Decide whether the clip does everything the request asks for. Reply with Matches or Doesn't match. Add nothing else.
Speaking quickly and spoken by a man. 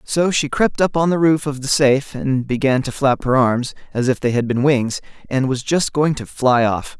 Matches